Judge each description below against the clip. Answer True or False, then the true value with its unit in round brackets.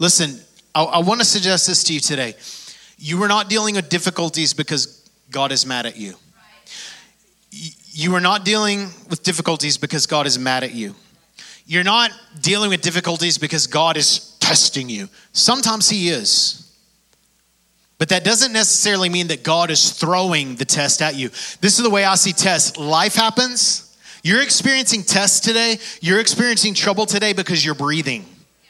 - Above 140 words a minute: True (170 wpm)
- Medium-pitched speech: True (180 Hz)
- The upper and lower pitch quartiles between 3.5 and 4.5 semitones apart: False (5.2 semitones)